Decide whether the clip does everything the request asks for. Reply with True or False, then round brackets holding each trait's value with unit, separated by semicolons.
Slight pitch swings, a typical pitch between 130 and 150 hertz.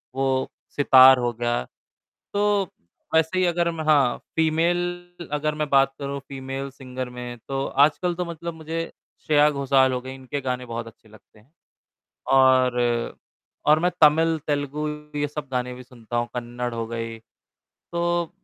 False (4.2 semitones; 140 Hz)